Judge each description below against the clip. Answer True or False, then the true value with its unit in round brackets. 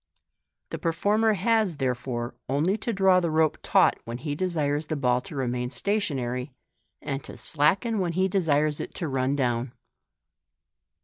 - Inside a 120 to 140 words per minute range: False (160 wpm)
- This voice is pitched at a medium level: True (150 Hz)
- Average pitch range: False (6.1 semitones)